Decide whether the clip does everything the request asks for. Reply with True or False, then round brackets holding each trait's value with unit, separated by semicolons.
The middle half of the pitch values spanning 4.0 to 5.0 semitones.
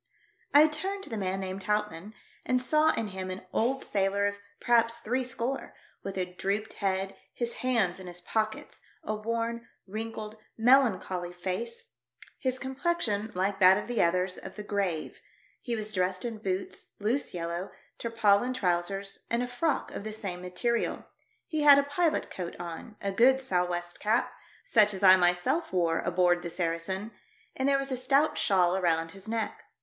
True (4.5 semitones)